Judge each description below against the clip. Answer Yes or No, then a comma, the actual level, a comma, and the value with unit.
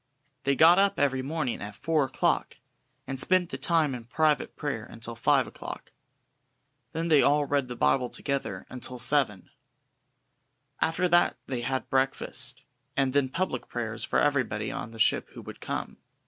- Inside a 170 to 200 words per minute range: No, average, 160 wpm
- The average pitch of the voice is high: No, low, 135 Hz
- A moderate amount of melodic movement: Yes, average, 3.8 semitones